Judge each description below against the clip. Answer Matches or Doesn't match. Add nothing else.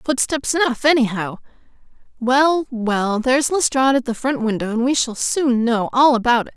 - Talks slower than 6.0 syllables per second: Matches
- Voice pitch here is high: Matches